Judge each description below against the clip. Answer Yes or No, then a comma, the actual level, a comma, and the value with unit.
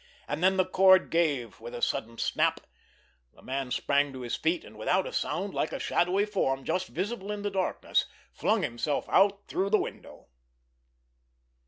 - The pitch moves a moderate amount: No, wide, 6.4 semitones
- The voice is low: No, medium, 180 Hz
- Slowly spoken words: No, average, 175 wpm